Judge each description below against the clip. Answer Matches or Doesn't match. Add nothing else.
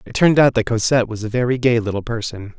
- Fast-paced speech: Matches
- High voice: Doesn't match